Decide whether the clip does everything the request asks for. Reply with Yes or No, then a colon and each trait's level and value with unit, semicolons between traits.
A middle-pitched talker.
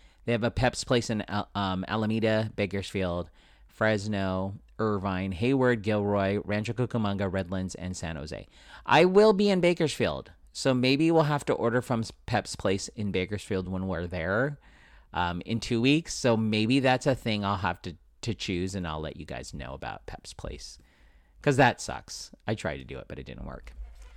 No: low, 100 Hz